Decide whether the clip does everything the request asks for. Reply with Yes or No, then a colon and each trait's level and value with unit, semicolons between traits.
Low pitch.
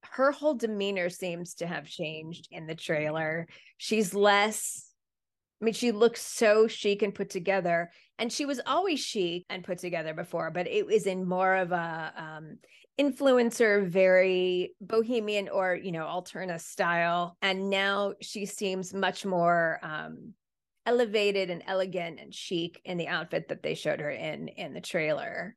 No: high, 190 Hz